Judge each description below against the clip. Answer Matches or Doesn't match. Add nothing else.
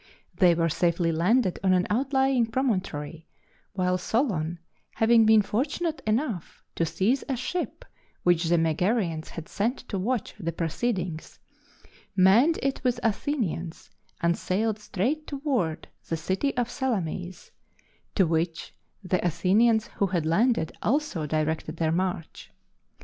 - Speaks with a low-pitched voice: Doesn't match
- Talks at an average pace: Doesn't match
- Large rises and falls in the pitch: Matches